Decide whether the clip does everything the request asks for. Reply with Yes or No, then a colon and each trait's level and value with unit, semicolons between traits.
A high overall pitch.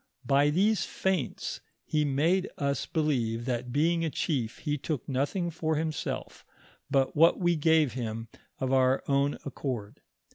No: medium, 145 Hz